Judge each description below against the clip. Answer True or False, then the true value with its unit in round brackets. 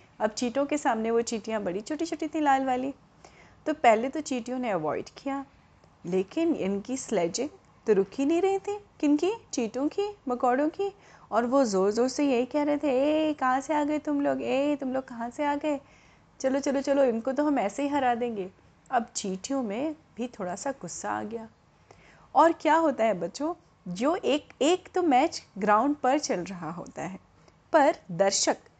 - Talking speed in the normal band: False (195 wpm)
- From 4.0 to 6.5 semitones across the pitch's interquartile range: True (4.6 semitones)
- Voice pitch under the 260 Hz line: False (270 Hz)